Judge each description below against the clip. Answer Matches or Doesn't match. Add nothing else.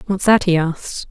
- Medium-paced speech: Doesn't match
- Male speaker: Doesn't match